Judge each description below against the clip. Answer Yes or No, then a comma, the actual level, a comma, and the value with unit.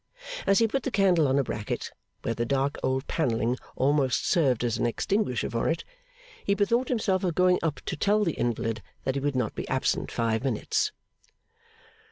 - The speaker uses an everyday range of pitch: No, wide, 7.8 semitones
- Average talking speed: Yes, average, 190 wpm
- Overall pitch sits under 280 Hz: Yes, medium, 140 Hz